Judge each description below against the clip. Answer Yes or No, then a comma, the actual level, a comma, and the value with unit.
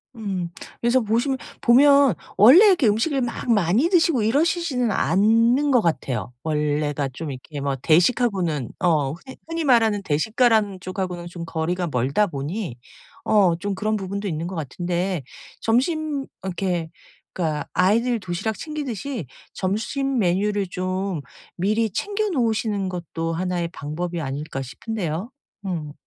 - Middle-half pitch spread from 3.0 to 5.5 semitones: No, wide, 6.0 semitones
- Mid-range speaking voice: No, high, 195 Hz